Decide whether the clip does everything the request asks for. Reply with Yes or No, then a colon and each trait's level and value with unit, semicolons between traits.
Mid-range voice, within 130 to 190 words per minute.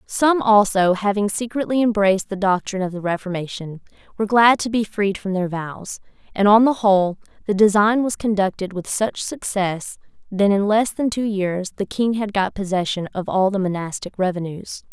No: high, 200 Hz; average, 180 wpm